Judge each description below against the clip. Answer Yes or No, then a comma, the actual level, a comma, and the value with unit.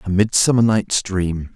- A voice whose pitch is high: No, low, 100 Hz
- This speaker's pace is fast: No, average, 155 wpm